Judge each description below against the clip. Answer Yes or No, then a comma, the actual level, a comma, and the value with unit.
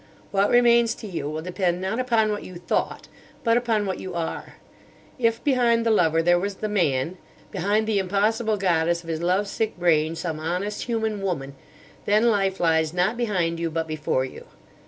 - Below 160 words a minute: No, average, 180 wpm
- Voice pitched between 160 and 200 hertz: Yes, high, 190 Hz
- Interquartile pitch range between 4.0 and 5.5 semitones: Yes, average, 4.7 semitones